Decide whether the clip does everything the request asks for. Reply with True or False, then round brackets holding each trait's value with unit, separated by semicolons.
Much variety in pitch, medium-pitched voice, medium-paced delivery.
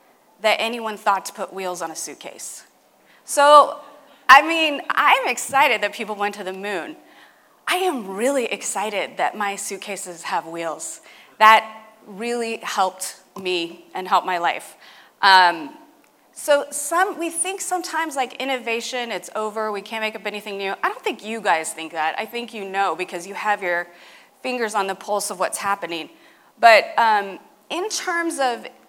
False (6.6 semitones; 220 Hz; 165 wpm)